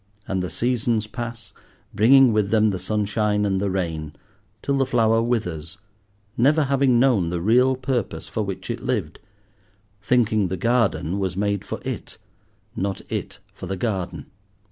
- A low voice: Yes, low, 105 Hz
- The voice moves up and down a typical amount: Yes, average, 4.1 semitones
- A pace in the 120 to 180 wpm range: Yes, average, 155 wpm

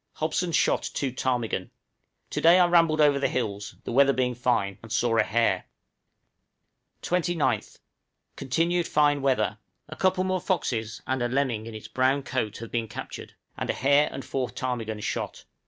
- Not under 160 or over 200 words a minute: Yes, average, 170 wpm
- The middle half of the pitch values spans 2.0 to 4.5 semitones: No, average, 5.0 semitones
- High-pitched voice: No, low, 130 Hz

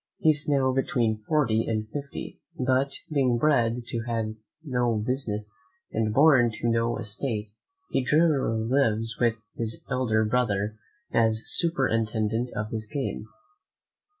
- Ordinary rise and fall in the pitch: Yes, average, 3.3 semitones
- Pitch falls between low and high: No, low, 115 Hz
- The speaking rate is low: Yes, slow, 125 wpm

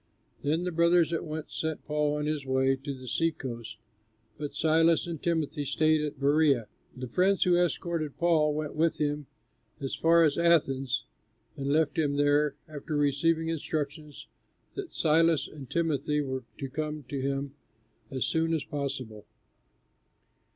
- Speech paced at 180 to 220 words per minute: No, average, 155 wpm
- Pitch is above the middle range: No, medium, 150 Hz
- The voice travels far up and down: No, average, 2.8 semitones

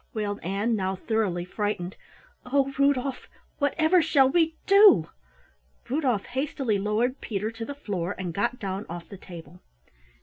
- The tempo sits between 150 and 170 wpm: No, average, 140 wpm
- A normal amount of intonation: No, wide, 6.2 semitones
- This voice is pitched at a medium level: No, high, 220 Hz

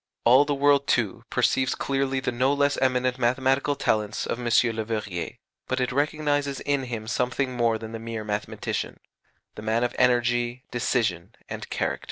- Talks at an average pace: Yes, average, 165 wpm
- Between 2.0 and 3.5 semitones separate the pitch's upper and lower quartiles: Yes, average, 2.9 semitones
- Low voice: Yes, low, 125 Hz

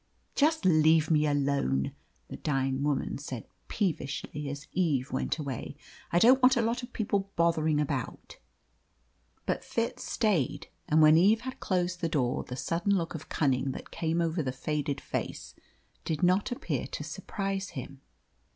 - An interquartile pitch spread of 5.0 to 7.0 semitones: Yes, average, 5.3 semitones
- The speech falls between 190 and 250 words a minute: No, average, 160 wpm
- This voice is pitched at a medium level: Yes, medium, 160 Hz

